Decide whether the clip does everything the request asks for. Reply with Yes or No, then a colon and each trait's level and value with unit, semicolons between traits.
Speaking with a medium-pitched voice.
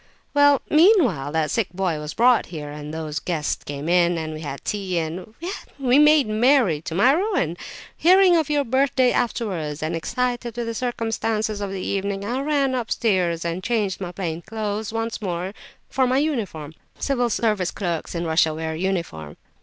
No: high, 200 Hz